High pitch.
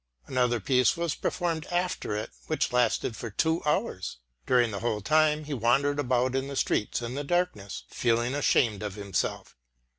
No: low, 125 Hz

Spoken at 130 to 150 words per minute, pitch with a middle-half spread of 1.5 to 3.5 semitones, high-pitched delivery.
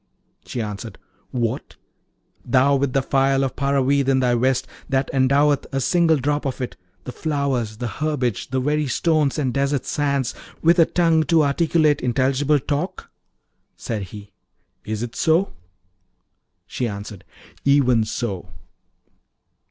No: slow, 135 wpm; average, 3.1 semitones; low, 135 Hz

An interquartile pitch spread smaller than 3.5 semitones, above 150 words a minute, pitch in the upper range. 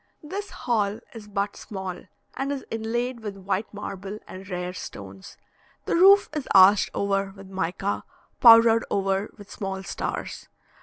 No: average, 3.1 semitones; average, 145 wpm; high, 200 Hz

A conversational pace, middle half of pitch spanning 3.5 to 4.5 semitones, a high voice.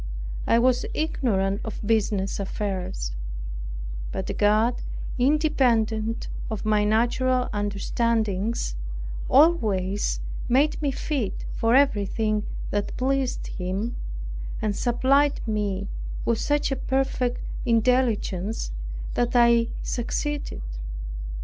No: slow, 90 wpm; average, 3.9 semitones; high, 230 Hz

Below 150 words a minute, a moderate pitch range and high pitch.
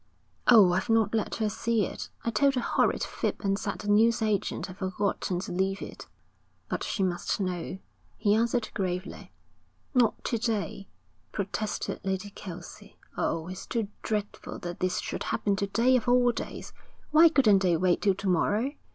No: average, 170 wpm; average, 3.3 semitones; high, 205 Hz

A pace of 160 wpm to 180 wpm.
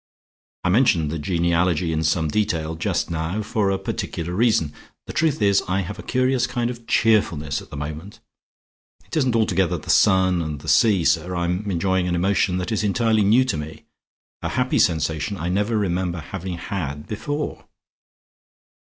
Yes: average, 175 wpm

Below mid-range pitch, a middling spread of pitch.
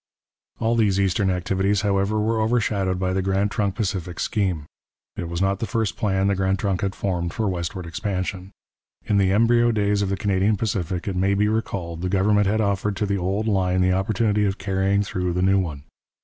No: very low, 95 Hz; narrow, 1.9 semitones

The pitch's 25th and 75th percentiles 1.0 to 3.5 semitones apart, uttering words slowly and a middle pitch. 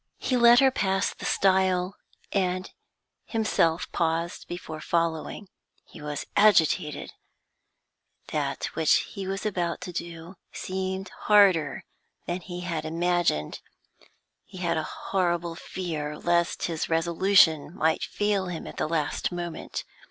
Yes: average, 2.7 semitones; slow, 120 wpm; medium, 175 Hz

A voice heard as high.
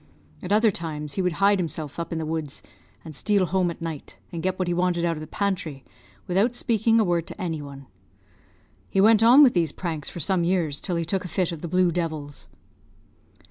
No: medium, 175 Hz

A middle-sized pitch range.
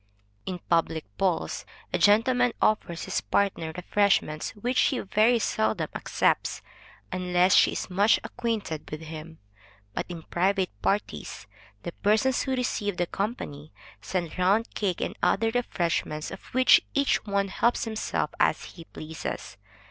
Yes: average, 4.5 semitones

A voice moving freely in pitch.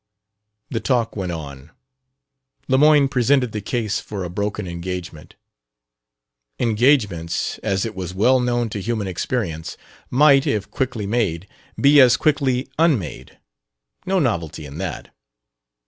Yes: wide, 6.2 semitones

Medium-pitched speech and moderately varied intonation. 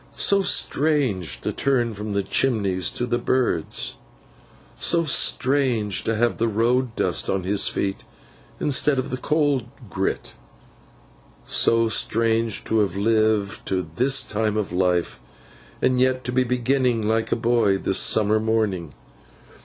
No: low, 115 Hz; average, 3.9 semitones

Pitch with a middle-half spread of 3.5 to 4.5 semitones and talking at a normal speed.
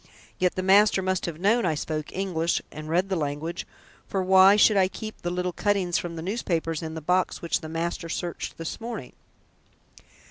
No: average, 2.9 semitones; average, 190 wpm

